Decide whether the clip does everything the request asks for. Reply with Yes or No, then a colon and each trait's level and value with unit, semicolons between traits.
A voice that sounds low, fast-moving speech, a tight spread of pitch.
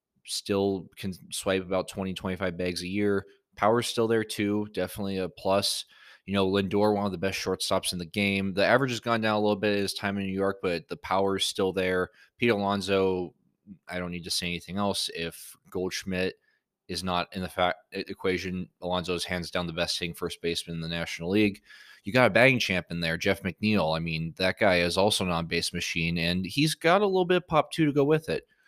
Yes: very low, 95 Hz; fast, 220 wpm; narrow, 2.3 semitones